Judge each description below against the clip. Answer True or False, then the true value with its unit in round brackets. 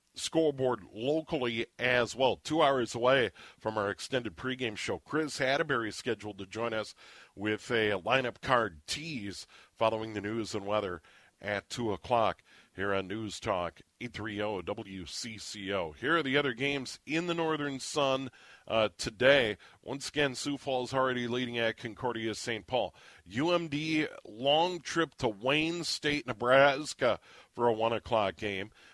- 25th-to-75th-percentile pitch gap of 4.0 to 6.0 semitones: True (4.7 semitones)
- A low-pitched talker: True (120 Hz)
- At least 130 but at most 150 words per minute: True (145 wpm)